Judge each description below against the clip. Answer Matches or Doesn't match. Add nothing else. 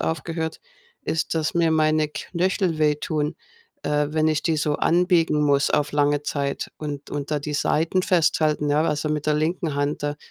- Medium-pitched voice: Matches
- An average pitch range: Doesn't match